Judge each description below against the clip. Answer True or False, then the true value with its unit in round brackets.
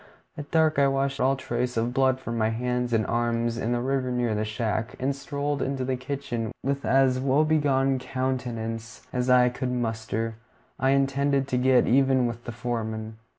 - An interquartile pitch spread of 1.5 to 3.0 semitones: True (2.6 semitones)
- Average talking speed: True (185 wpm)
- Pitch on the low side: True (125 Hz)